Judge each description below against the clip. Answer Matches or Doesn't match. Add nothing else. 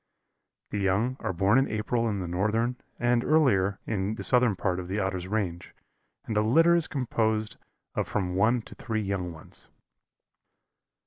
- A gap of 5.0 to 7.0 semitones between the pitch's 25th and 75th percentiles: Doesn't match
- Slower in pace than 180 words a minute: Matches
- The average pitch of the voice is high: Doesn't match